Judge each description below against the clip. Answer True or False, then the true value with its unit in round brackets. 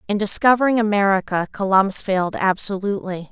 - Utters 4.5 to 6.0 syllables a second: False (6.2 syllables/s)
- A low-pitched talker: False (200 Hz)